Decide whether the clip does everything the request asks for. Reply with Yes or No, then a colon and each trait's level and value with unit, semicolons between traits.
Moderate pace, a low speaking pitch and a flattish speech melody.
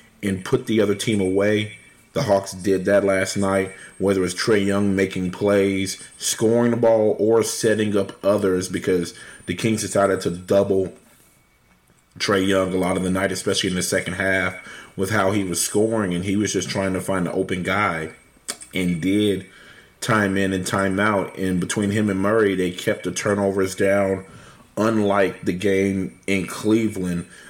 Yes: average, 175 wpm; very low, 95 Hz; narrow, 1.8 semitones